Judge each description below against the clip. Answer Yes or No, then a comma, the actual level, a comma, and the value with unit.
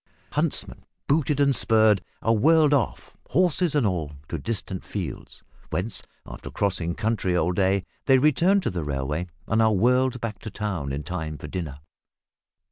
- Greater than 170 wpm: No, average, 160 wpm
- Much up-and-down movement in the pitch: Yes, wide, 6.9 semitones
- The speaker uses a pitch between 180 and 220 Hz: No, low, 105 Hz